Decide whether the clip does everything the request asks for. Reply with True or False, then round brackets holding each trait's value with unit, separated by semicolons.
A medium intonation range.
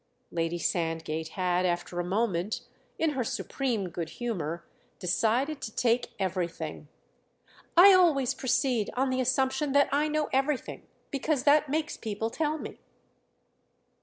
False (8.0 semitones)